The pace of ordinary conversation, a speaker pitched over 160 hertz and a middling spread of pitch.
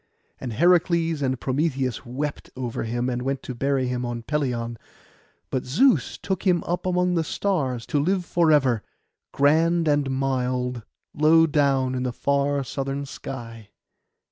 No: average, 150 wpm; low, 135 Hz; average, 4.3 semitones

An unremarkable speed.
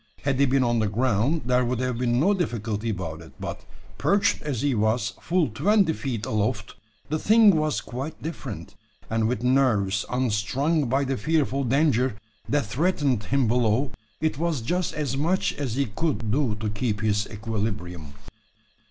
Yes: average, 170 wpm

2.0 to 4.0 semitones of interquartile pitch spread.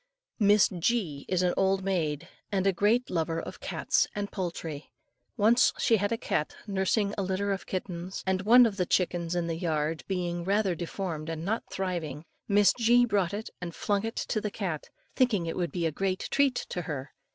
Yes: average, 3.3 semitones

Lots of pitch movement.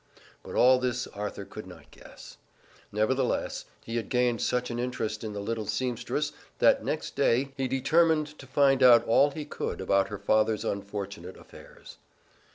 No: average, 3.8 semitones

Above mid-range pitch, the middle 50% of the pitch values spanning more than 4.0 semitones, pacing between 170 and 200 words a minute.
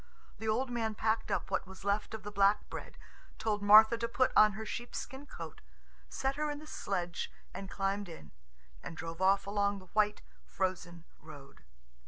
No: high, 205 Hz; average, 2.8 semitones; average, 180 wpm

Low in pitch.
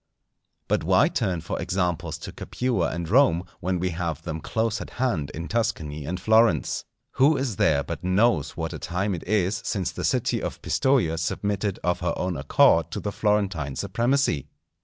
Yes: very low, 90 Hz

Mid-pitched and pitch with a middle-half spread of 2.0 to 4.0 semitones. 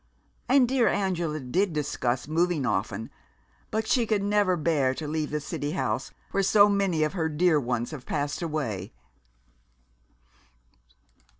No: medium, 155 Hz; wide, 5.5 semitones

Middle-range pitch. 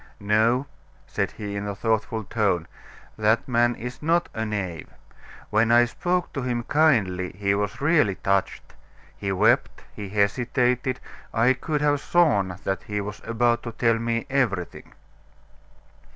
No: low, 115 Hz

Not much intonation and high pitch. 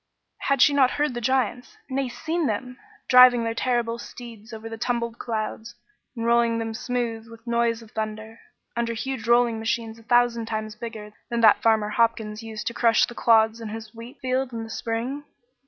Yes: narrow, 1.6 semitones; high, 230 Hz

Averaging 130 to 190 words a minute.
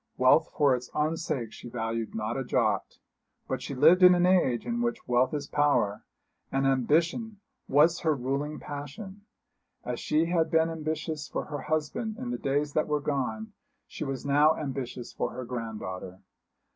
Yes: average, 170 wpm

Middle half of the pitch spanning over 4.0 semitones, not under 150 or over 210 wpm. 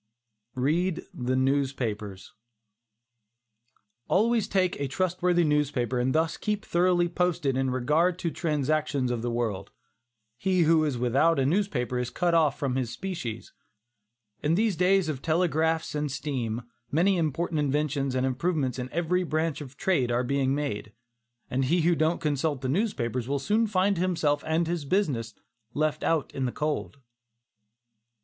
Yes: average, 4.9 semitones; average, 155 wpm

